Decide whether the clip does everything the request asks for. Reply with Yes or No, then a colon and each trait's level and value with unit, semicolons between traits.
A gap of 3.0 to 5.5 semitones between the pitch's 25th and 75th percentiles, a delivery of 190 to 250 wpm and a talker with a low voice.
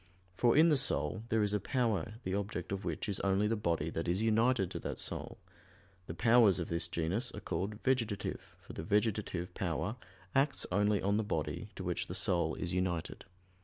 Yes: average, 4.0 semitones; average, 200 wpm; low, 100 Hz